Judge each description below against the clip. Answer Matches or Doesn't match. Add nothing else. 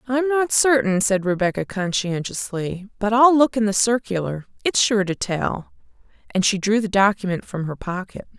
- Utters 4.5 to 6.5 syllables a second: Matches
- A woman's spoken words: Matches